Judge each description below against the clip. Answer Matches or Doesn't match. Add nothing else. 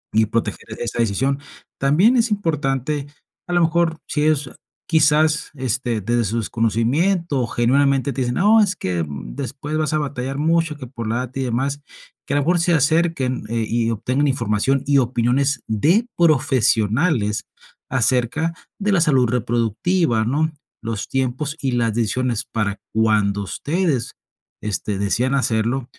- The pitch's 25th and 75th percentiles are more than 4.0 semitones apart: Matches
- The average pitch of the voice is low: Matches